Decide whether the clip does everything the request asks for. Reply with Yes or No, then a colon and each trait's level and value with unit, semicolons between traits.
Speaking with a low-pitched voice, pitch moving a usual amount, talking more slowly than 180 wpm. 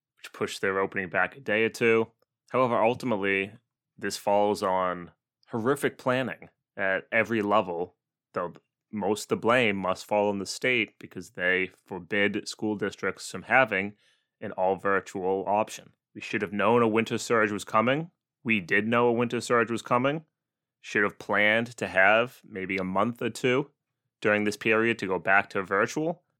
Yes: low, 110 Hz; average, 3.4 semitones; average, 170 wpm